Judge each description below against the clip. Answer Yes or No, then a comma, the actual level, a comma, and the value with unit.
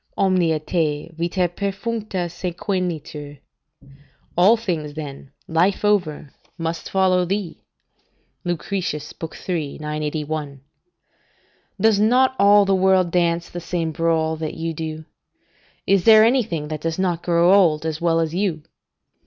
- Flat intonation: No, average, 3.3 semitones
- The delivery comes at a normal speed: No, slow, 125 wpm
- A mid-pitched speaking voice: Yes, medium, 170 Hz